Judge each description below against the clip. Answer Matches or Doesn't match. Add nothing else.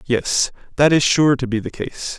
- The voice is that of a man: Matches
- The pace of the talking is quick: Matches